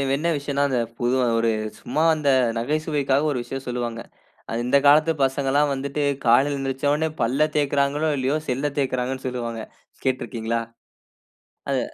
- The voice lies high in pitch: No, low, 135 Hz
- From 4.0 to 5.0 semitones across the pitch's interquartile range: No, narrow, 2.6 semitones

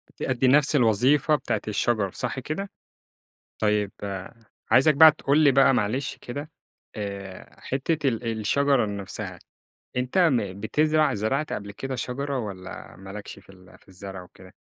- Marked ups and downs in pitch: Yes, wide, 5.7 semitones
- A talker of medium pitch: No, low, 125 Hz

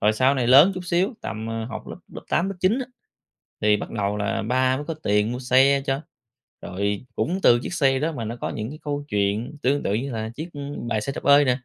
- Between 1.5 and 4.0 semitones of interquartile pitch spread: No, average, 5.0 semitones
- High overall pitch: No, low, 130 Hz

